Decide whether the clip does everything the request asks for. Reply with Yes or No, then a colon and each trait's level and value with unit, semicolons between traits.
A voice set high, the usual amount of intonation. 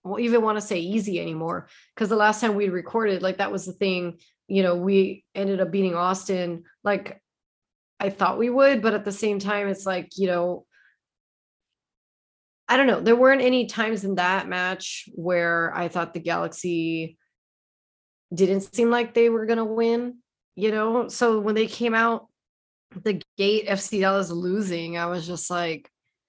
Yes: high, 195 Hz; average, 3.7 semitones